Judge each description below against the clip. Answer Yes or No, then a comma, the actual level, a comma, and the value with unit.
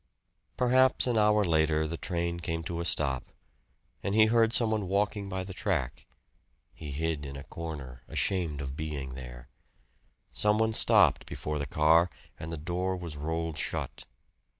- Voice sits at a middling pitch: No, very low, 85 Hz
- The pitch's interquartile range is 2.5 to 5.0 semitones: Yes, average, 4.7 semitones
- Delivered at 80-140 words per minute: No, average, 165 wpm